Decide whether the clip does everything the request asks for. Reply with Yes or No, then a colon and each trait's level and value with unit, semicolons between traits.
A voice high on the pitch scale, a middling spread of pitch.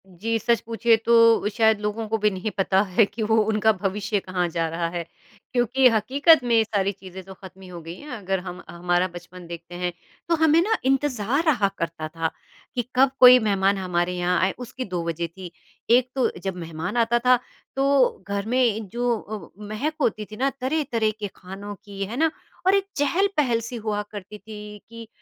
Yes: high, 215 Hz; average, 4.7 semitones